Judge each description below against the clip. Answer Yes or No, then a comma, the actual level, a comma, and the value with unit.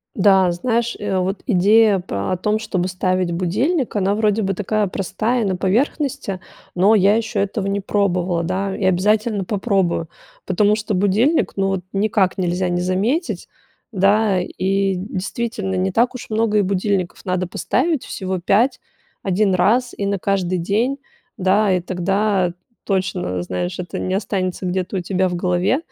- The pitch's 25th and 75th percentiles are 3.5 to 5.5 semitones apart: No, average, 2.7 semitones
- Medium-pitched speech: No, high, 195 Hz